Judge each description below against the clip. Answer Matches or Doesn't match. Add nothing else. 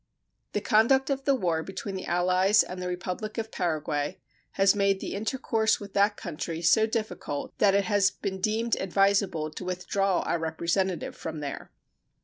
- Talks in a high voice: Matches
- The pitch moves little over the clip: Doesn't match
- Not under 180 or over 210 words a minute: Doesn't match